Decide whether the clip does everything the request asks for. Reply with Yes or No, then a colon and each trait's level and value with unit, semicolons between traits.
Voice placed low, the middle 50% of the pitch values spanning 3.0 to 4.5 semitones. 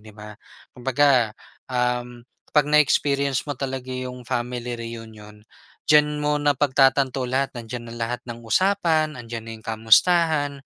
Yes: low, 125 Hz; average, 3.5 semitones